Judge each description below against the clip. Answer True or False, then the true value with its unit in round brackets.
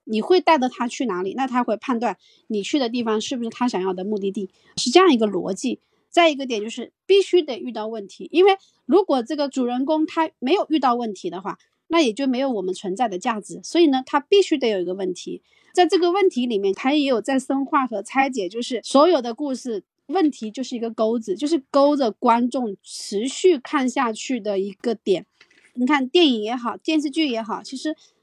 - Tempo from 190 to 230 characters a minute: False (315 characters per minute)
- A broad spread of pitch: True (6.1 semitones)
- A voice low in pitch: False (255 Hz)